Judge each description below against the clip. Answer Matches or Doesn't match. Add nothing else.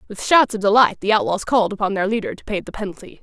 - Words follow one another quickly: Matches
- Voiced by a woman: Matches